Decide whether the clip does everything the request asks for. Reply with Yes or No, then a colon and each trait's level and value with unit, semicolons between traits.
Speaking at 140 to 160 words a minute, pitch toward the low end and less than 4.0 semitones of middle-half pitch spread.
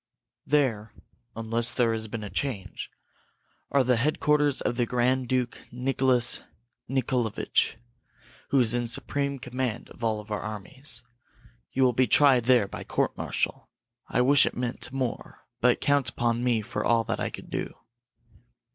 Yes: average, 155 wpm; low, 125 Hz; narrow, 2.5 semitones